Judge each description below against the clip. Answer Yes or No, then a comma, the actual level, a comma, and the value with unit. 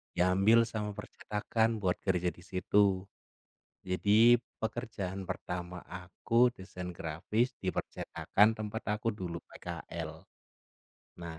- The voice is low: Yes, low, 100 Hz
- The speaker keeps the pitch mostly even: No, average, 3.6 semitones